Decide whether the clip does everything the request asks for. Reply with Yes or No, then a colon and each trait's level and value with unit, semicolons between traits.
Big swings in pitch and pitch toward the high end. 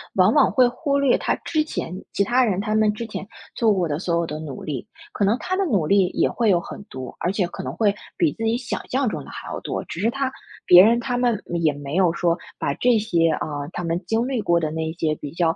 Yes: wide, 6.0 semitones; high, 195 Hz